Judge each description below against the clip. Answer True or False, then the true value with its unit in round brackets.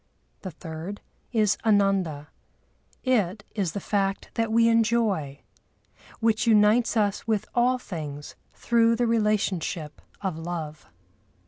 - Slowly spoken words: True (115 wpm)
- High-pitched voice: True (205 Hz)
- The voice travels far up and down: False (5.0 semitones)